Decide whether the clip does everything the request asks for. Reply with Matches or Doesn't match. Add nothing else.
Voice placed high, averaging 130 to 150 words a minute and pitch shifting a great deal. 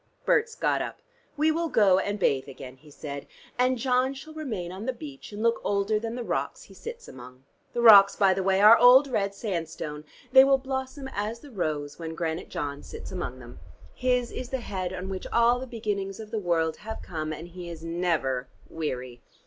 Doesn't match